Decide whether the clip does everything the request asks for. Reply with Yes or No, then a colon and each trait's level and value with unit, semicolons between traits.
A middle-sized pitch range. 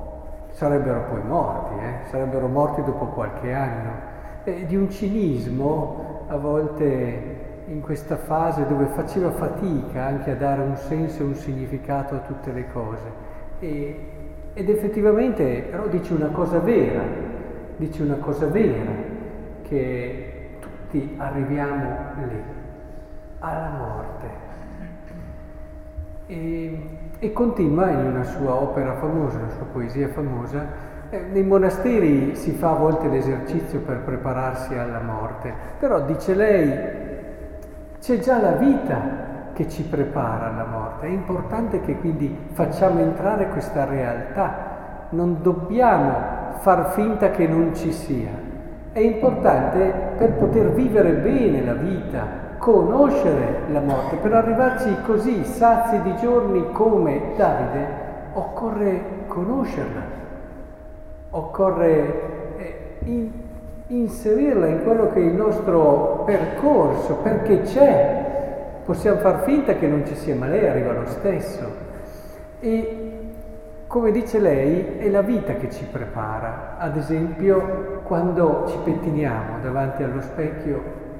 No: wide, 6.1 semitones